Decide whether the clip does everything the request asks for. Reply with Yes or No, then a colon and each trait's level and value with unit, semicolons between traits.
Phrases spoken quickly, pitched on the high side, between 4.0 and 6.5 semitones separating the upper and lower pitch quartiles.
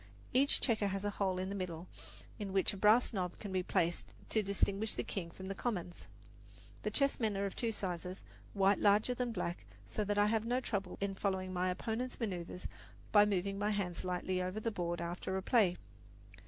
No: fast, 210 wpm; high, 195 Hz; narrow, 2.6 semitones